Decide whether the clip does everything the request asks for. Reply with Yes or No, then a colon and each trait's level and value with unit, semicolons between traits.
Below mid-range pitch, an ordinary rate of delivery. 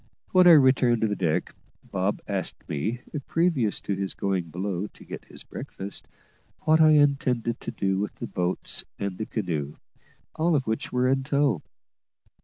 Yes: low, 110 Hz; average, 170 wpm